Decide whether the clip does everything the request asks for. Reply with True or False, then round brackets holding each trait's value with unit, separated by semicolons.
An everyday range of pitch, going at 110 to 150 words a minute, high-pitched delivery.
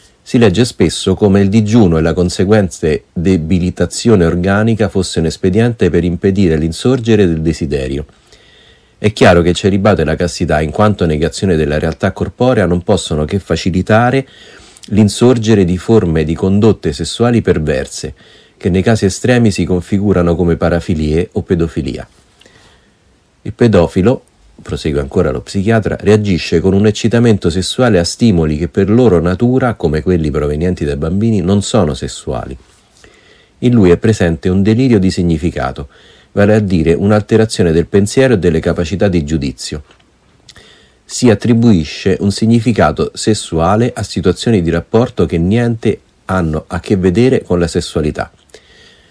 False (4.5 semitones; 140 wpm; 95 Hz)